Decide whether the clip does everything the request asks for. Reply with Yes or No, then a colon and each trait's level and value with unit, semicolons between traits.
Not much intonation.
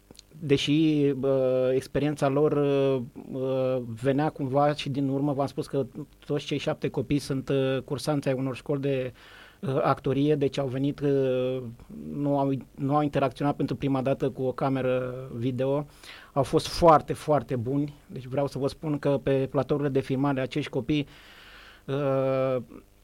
Yes: narrow, 1.7 semitones